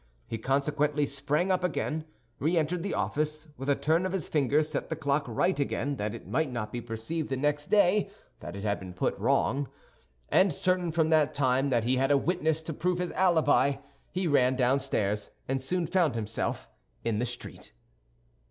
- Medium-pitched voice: Yes, medium, 145 Hz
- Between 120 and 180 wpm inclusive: No, average, 190 wpm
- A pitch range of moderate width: Yes, average, 4.3 semitones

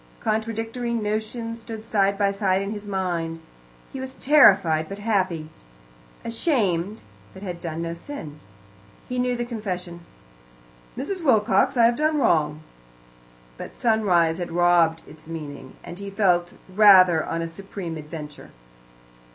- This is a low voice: No, high, 195 Hz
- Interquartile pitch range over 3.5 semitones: Yes, average, 5.2 semitones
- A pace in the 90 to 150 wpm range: Yes, slow, 135 wpm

